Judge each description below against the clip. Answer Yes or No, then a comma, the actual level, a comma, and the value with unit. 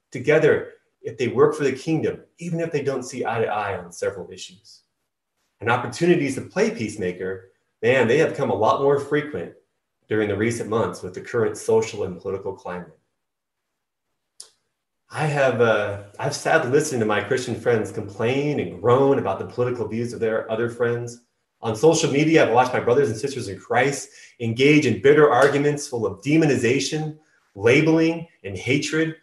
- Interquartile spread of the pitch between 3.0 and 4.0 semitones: No, average, 5.3 semitones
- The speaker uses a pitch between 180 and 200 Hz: No, medium, 140 Hz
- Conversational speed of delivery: Yes, average, 170 wpm